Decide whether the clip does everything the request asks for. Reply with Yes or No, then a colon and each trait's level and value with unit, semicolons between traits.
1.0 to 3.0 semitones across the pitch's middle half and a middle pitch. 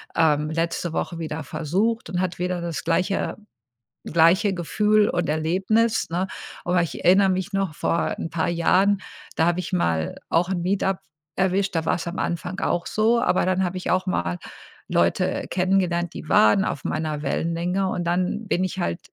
Yes: narrow, 2.4 semitones; medium, 180 Hz